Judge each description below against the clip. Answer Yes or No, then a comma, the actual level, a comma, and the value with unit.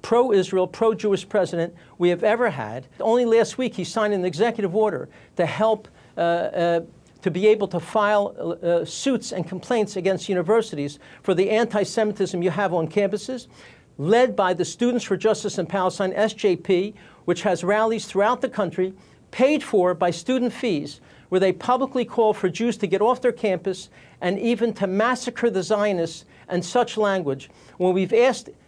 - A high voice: Yes, high, 200 Hz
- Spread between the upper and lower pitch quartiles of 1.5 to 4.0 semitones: Yes, average, 3.6 semitones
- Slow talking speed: No, average, 175 wpm